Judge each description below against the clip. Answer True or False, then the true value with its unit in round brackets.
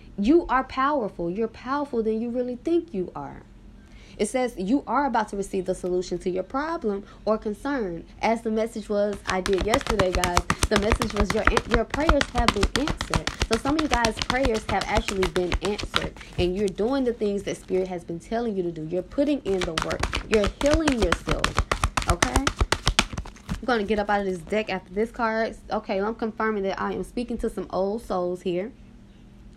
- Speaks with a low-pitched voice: False (215 Hz)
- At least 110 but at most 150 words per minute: False (200 wpm)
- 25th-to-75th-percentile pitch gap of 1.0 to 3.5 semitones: False (4.1 semitones)